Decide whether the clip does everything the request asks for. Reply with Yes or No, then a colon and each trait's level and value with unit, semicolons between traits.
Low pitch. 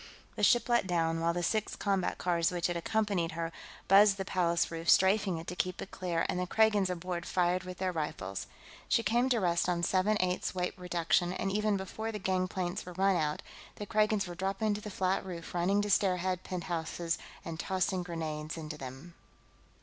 No: medium, 180 Hz